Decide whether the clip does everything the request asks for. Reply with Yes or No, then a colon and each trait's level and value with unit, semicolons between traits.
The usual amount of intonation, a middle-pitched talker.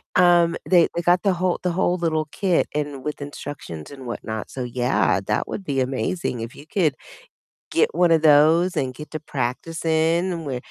Yes: average, 4.8 semitones; medium, 155 Hz